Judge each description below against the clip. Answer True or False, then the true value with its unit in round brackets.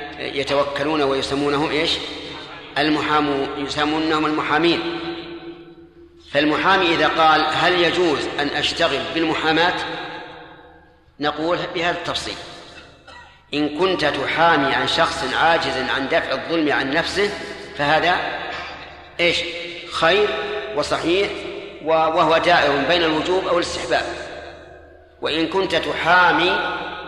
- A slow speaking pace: False (90 wpm)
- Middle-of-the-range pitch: True (160 Hz)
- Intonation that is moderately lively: True (3.5 semitones)